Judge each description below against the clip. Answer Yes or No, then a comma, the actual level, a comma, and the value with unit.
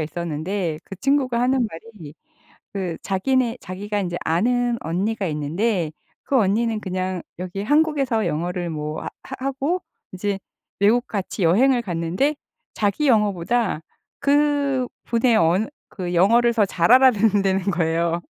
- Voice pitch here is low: No, high, 205 Hz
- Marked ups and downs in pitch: Yes, wide, 5.7 semitones